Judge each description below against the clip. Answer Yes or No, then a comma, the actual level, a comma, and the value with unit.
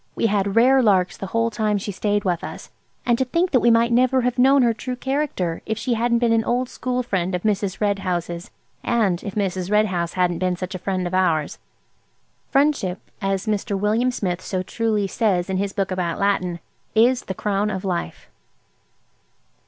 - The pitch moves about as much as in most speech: Yes, average, 4.2 semitones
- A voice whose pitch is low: No, high, 205 Hz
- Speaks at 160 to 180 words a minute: No, average, 200 wpm